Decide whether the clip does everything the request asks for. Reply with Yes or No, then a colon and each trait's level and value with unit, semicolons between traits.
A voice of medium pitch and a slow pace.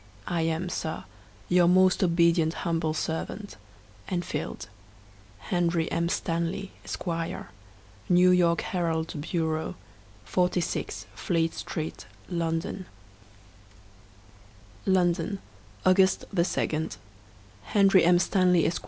Yes: medium, 170 Hz; slow, 90 wpm